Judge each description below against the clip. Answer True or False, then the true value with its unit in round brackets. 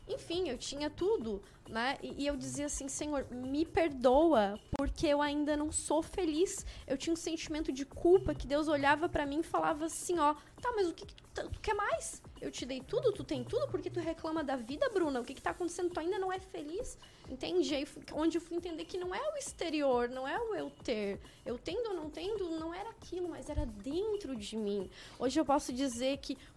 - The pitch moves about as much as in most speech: True (4.3 semitones)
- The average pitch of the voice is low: False (315 Hz)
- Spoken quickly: True (225 wpm)